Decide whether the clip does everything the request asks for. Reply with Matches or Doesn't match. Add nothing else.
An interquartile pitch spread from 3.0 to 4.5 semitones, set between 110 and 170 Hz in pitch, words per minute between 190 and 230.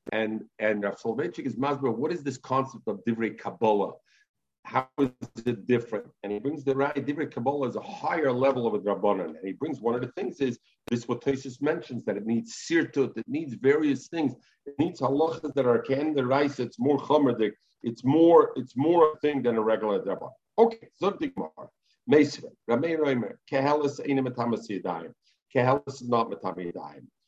Doesn't match